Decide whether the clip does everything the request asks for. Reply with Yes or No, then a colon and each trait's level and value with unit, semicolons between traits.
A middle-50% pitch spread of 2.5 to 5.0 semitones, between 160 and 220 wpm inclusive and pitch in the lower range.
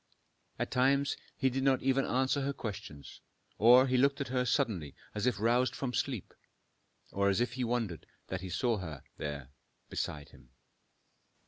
No: wide, 5.6 semitones; average, 165 wpm; low, 120 Hz